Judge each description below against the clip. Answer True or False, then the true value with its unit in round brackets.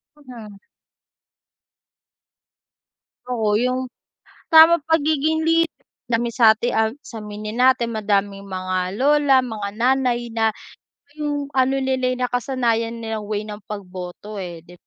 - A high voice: True (235 Hz)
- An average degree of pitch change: True (3.9 semitones)